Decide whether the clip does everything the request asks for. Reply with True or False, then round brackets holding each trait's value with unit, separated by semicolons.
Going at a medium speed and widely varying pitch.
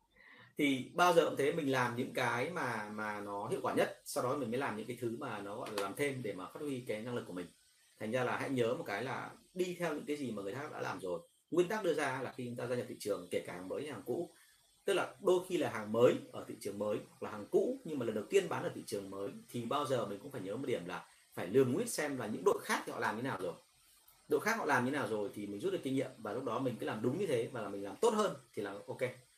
False (320 wpm; 6.4 semitones)